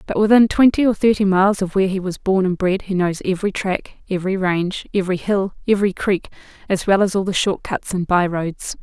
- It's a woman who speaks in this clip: Yes, female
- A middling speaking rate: No, fast, 225 wpm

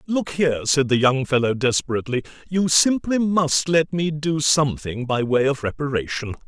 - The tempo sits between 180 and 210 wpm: No, average, 165 wpm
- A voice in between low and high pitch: Yes, medium, 145 Hz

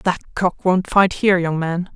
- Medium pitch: Yes, medium, 180 Hz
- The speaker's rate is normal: No, fast, 215 wpm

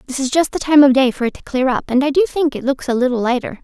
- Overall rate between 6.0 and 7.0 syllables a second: Yes, 6.9 syllables/s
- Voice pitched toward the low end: No, very high, 270 Hz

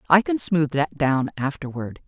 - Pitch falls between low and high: Yes, medium, 150 Hz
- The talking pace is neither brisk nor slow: Yes, average, 175 wpm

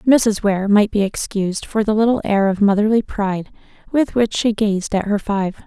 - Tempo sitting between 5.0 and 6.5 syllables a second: No, 4.8 syllables/s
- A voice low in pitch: No, high, 210 Hz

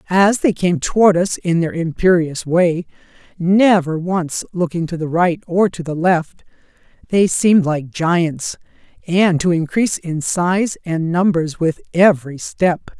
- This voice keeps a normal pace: Yes, average, 150 wpm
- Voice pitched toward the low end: No, medium, 175 Hz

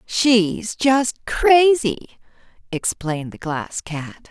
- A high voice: Yes, high, 220 Hz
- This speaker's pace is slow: Yes, slow, 100 wpm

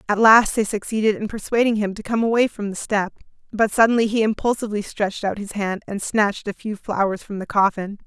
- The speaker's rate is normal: No, fast, 215 wpm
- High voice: Yes, high, 210 Hz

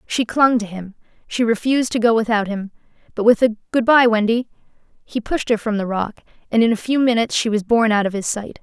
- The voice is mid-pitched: No, high, 225 Hz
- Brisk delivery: Yes, fast, 235 wpm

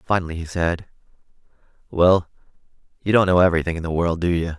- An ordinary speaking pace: Yes, average, 170 wpm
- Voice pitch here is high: No, very low, 85 Hz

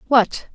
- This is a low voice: No, high, 235 Hz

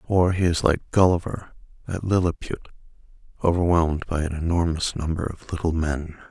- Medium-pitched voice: No, very low, 85 Hz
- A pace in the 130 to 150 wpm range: Yes, average, 145 wpm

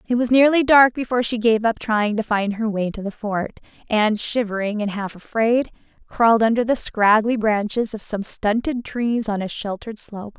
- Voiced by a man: No, female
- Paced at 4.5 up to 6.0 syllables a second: Yes, 5.0 syllables/s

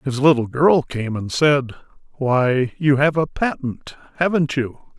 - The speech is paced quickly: No, average, 155 wpm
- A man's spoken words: Yes, male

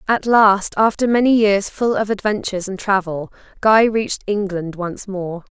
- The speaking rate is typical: Yes, average, 160 wpm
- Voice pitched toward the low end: No, high, 205 Hz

